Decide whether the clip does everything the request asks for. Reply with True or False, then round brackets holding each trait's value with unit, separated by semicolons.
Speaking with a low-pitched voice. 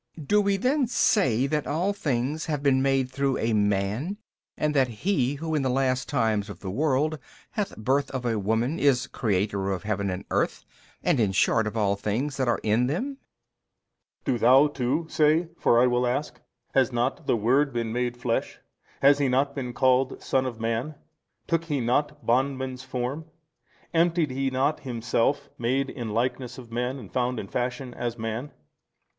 True (130 Hz)